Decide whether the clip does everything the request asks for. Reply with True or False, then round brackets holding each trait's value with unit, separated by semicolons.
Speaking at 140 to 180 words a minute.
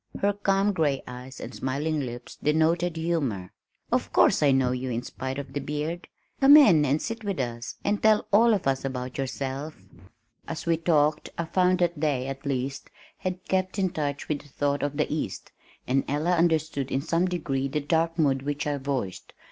False (195 wpm)